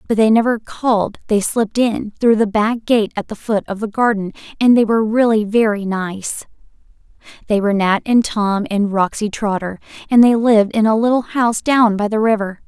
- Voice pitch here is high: Yes, high, 215 Hz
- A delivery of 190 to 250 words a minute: Yes, average, 200 wpm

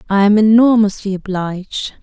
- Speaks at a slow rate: Yes, slow, 120 wpm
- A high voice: Yes, high, 205 Hz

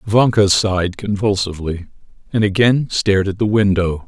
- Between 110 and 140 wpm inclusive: Yes, slow, 135 wpm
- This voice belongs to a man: Yes, male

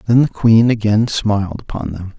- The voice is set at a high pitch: No, low, 105 Hz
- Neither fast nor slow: Yes, average, 190 wpm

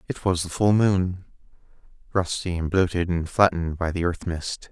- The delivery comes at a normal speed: Yes, average, 180 wpm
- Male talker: Yes, male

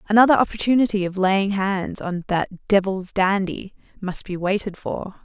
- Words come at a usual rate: Yes, average, 150 wpm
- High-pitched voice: Yes, high, 195 Hz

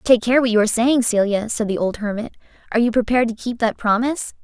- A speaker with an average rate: No, fast, 245 wpm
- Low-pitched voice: No, high, 230 Hz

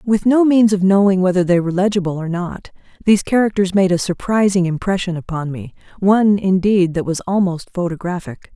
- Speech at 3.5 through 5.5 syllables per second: No, 5.7 syllables/s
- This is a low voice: No, high, 190 Hz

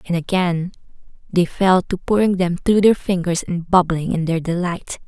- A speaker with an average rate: Yes, average, 175 wpm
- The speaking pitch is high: No, medium, 180 Hz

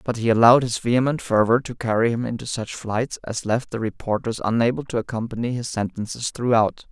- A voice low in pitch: Yes, low, 115 Hz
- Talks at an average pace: Yes, average, 190 wpm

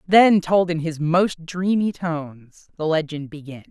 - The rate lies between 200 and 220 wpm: No, average, 160 wpm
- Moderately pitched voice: Yes, medium, 165 Hz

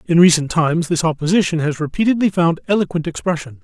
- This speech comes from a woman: No, male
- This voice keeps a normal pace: Yes, average, 165 wpm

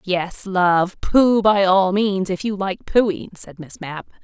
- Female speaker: Yes, female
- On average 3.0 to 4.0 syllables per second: Yes, 3.5 syllables/s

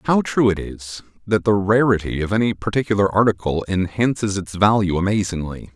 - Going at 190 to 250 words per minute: No, average, 155 wpm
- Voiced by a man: Yes, male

